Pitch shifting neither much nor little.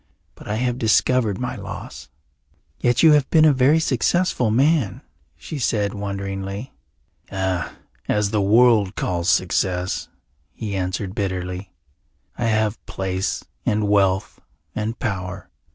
Yes: average, 4.2 semitones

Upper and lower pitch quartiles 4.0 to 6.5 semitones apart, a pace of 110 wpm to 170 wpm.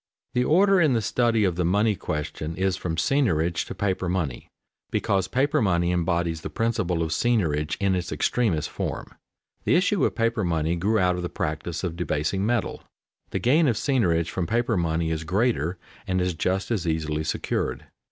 No: wide, 5.4 semitones; average, 185 wpm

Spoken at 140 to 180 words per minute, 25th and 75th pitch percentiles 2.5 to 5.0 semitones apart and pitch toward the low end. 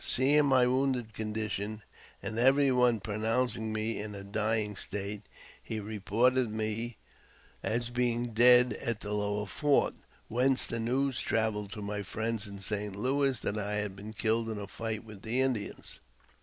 Yes: average, 170 wpm; average, 2.9 semitones; low, 110 Hz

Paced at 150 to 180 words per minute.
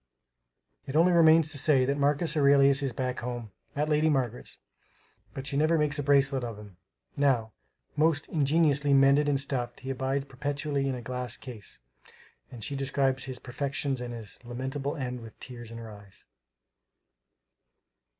Yes: average, 160 wpm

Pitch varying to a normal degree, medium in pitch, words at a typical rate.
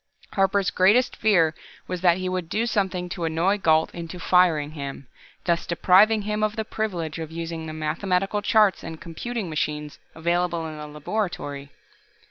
Yes: average, 3.8 semitones; medium, 175 Hz; average, 160 wpm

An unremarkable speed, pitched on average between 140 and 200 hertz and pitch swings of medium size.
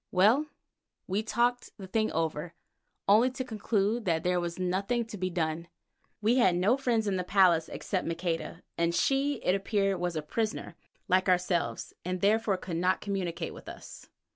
Yes: average, 170 wpm; high, 190 Hz; average, 3.8 semitones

